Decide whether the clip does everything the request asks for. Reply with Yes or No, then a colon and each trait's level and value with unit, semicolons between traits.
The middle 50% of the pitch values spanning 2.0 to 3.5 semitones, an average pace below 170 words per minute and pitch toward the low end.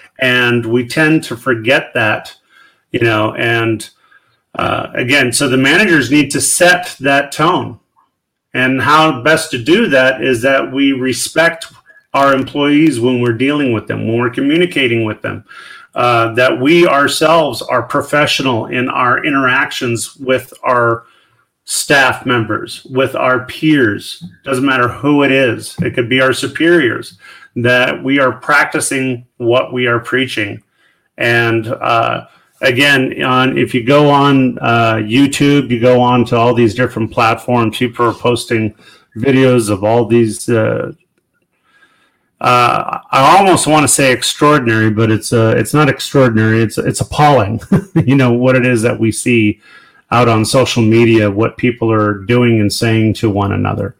Yes: average, 3.2 semitones; average, 155 wpm; low, 125 Hz